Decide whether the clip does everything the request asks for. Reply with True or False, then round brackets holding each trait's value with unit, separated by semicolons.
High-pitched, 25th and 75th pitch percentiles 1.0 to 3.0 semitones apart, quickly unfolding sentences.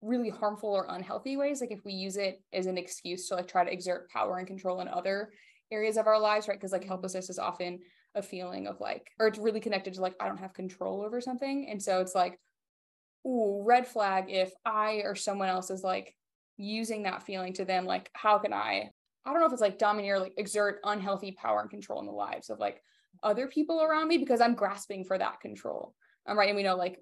True (200 Hz; 2.5 semitones; 240 wpm)